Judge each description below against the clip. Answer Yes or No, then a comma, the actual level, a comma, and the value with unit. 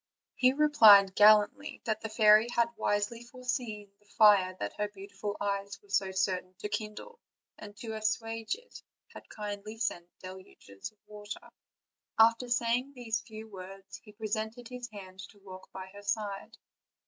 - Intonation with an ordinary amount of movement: No, narrow, 2.3 semitones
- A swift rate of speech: No, average, 155 wpm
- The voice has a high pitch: Yes, high, 210 Hz